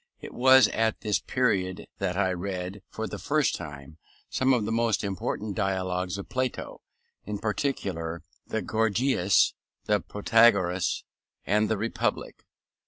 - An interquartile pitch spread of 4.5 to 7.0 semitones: No, average, 3.5 semitones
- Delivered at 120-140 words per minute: Yes, slow, 135 wpm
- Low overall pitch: Yes, low, 105 Hz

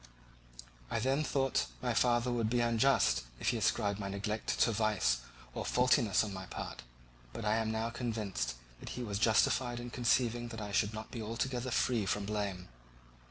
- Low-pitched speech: Yes, low, 110 Hz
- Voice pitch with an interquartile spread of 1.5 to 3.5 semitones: Yes, average, 2.8 semitones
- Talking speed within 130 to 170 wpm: No, average, 185 wpm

